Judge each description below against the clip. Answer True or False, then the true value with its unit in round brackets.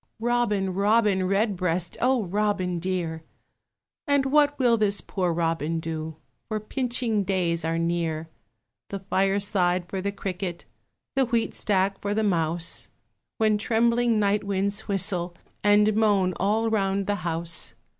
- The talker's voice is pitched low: False (195 Hz)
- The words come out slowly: True (130 wpm)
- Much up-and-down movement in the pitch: False (3.4 semitones)